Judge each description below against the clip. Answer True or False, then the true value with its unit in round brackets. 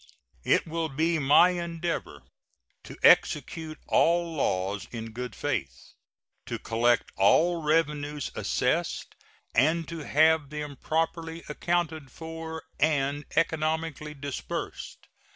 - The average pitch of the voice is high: False (155 Hz)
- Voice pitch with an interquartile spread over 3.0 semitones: False (2.6 semitones)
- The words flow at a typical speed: False (105 wpm)